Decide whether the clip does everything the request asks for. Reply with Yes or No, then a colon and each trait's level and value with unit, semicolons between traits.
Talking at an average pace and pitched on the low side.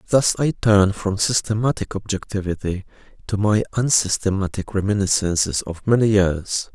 No: slow, 115 wpm; low, 100 Hz